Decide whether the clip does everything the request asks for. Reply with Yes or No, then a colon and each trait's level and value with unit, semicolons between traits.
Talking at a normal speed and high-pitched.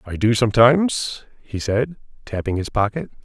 No: average, 150 wpm; low, 115 Hz